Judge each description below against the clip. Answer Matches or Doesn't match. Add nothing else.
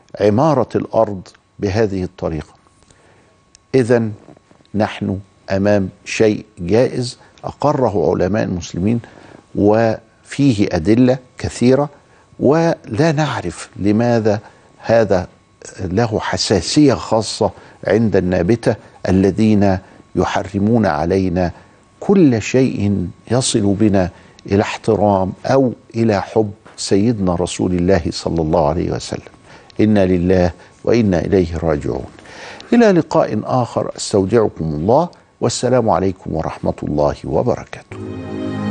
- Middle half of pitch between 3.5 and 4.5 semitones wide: Matches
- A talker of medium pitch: Doesn't match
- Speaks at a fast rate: Doesn't match